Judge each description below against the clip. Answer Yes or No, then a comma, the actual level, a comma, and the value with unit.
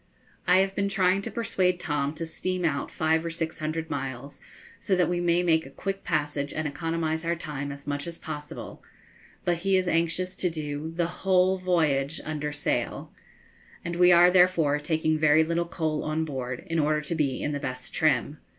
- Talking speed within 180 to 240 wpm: Yes, average, 195 wpm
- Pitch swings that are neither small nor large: Yes, average, 3.1 semitones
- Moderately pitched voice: Yes, medium, 160 Hz